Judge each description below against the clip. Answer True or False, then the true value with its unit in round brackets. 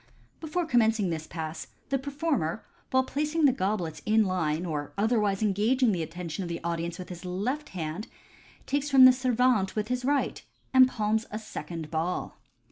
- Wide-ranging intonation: True (7.1 semitones)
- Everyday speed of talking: True (175 wpm)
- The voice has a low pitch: False (210 Hz)